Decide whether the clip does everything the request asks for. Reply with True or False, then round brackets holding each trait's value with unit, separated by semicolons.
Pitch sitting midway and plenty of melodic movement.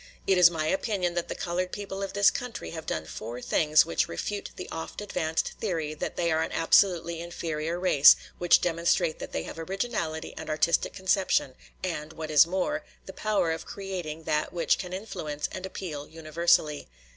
False (170 Hz; 3.2 semitones)